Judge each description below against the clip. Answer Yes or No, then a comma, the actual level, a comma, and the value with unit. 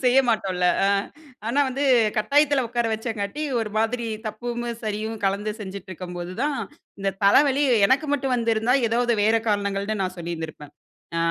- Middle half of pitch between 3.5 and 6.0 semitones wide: Yes, average, 3.9 semitones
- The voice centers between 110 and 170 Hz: No, high, 220 Hz